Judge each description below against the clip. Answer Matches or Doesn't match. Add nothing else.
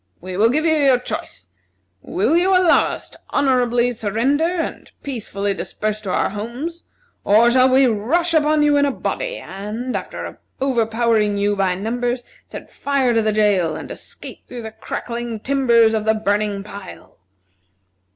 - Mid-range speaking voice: Doesn't match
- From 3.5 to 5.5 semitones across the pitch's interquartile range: Matches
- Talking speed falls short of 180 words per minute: Matches